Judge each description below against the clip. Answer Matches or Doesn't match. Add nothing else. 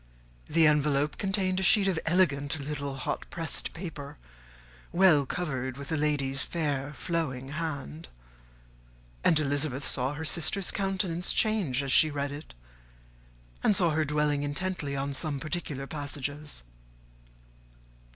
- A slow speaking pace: Matches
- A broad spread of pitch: Doesn't match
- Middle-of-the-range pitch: Matches